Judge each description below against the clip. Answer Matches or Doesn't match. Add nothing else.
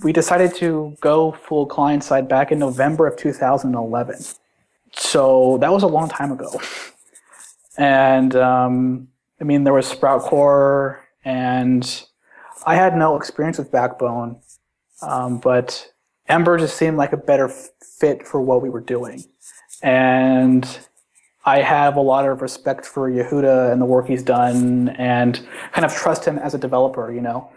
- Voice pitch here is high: Doesn't match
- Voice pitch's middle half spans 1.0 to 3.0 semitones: Matches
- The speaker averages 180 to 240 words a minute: Doesn't match